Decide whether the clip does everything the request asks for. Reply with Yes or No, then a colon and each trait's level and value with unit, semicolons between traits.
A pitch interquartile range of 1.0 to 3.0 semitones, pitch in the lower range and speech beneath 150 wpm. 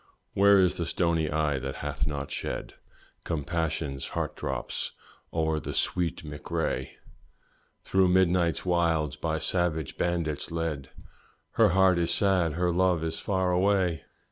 Yes: average, 2.7 semitones; very low, 85 Hz; average, 140 wpm